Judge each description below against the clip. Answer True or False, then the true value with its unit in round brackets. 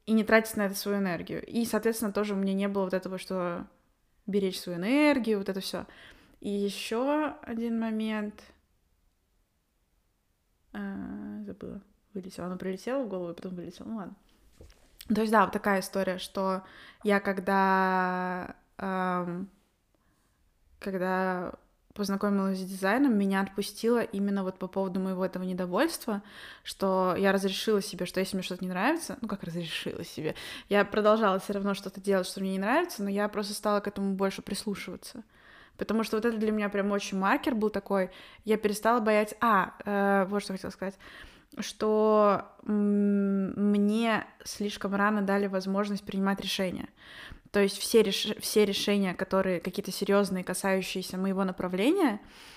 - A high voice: True (200 Hz)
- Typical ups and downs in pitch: False (2.1 semitones)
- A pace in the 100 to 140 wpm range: False (155 wpm)